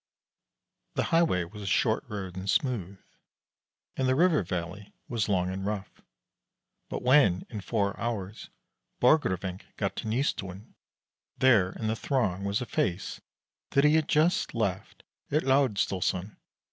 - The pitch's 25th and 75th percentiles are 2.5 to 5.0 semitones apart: No, wide, 5.4 semitones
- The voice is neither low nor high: No, low, 105 Hz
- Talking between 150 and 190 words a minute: No, average, 140 wpm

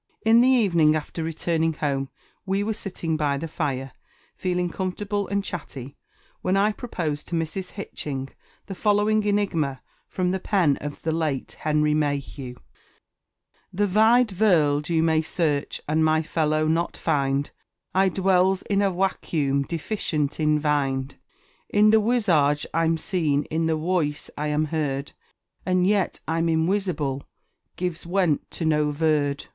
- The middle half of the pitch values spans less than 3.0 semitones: No, average, 4.3 semitones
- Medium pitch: Yes, medium, 160 Hz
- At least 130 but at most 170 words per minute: Yes, average, 145 wpm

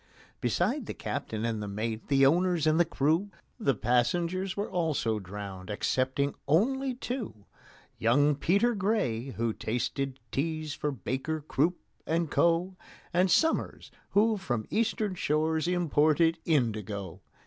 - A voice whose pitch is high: No, medium, 155 Hz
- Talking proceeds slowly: Yes, slow, 130 wpm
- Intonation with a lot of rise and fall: Yes, wide, 7.0 semitones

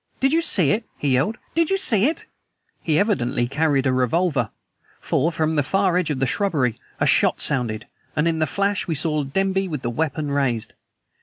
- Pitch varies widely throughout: Yes, wide, 6.3 semitones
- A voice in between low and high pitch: Yes, medium, 155 Hz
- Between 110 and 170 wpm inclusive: No, average, 195 wpm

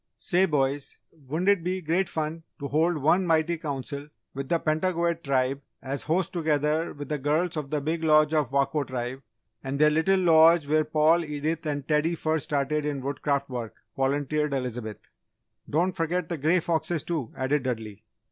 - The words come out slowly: No, average, 175 wpm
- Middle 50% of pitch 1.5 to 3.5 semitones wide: Yes, average, 2.9 semitones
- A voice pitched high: No, medium, 150 Hz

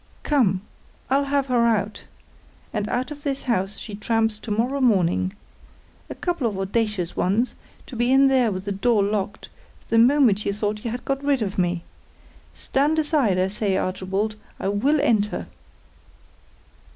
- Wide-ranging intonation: No, average, 4.8 semitones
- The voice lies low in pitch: No, high, 220 Hz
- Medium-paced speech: Yes, average, 165 wpm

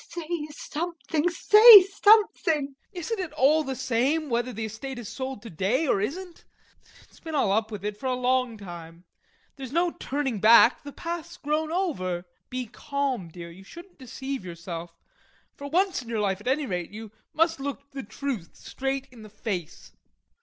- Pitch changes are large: Yes, wide, 6.7 semitones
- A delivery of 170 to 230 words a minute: Yes, average, 180 wpm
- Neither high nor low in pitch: No, very high, 265 Hz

